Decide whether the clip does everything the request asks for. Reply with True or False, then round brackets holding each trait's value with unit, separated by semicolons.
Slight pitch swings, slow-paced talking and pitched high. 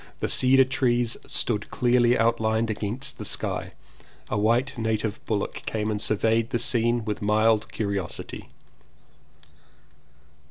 False (1.9 semitones; 125 wpm; 115 Hz)